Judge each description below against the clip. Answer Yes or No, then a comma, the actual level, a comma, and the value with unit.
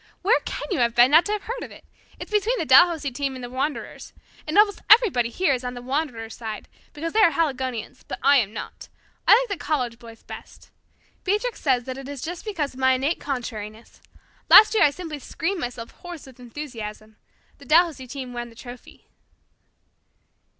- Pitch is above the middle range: Yes, very high, 275 Hz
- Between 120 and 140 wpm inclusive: No, average, 195 wpm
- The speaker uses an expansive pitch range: Yes, wide, 5.9 semitones